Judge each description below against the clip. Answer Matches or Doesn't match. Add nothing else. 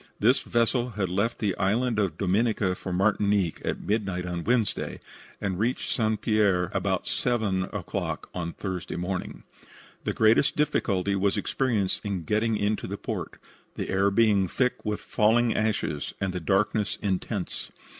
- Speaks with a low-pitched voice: Matches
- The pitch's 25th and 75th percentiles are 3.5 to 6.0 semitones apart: Doesn't match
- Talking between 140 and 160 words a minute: Matches